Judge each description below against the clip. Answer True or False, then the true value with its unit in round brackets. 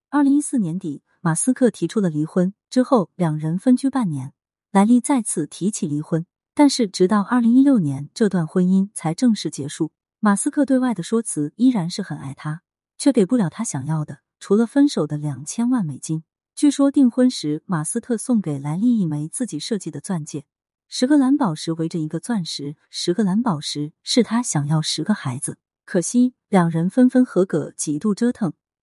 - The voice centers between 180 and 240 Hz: True (190 Hz)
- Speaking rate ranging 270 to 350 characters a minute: True (285 characters per minute)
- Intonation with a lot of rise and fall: True (7.6 semitones)